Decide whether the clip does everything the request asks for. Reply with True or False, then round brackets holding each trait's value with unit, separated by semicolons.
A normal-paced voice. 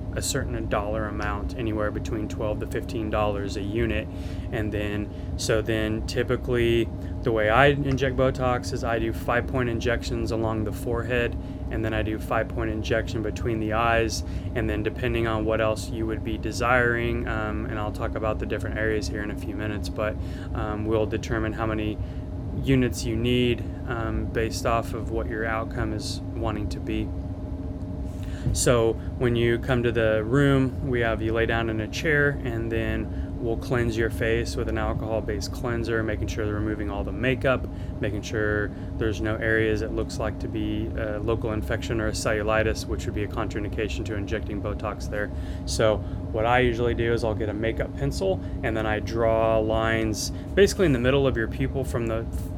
True (190 wpm)